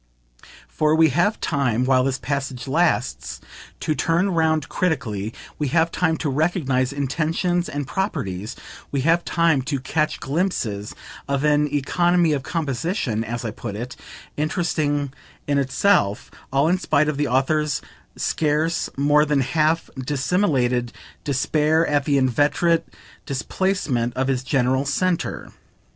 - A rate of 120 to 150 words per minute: Yes, slow, 135 wpm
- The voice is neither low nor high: Yes, medium, 145 Hz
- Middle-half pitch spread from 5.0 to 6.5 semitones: No, average, 3.8 semitones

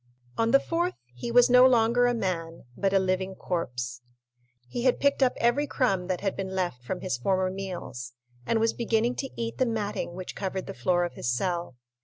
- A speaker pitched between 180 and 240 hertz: Yes, high, 190 Hz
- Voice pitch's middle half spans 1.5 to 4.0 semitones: No, average, 5.2 semitones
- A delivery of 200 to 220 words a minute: Yes, fast, 205 wpm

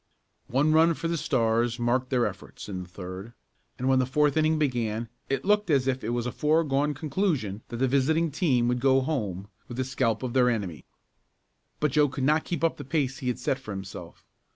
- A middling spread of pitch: Yes, average, 4.2 semitones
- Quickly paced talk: Yes, fast, 215 wpm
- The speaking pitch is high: No, low, 130 Hz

